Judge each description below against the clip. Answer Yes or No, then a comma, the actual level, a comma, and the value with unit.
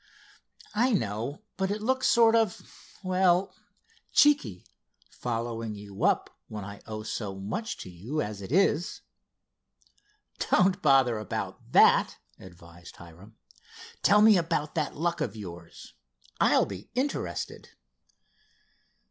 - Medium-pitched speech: No, low, 125 Hz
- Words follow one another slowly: Yes, slow, 115 wpm